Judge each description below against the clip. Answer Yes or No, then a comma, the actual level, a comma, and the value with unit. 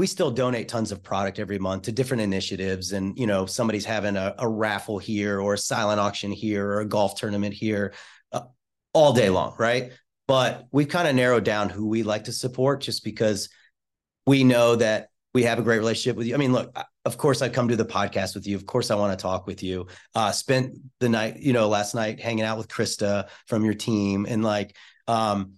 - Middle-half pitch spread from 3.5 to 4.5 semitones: No, average, 2.9 semitones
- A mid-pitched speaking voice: No, low, 110 Hz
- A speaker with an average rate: No, fast, 225 wpm